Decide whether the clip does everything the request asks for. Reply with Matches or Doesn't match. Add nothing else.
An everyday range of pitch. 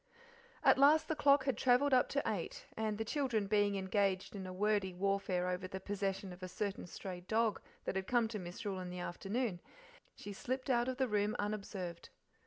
Matches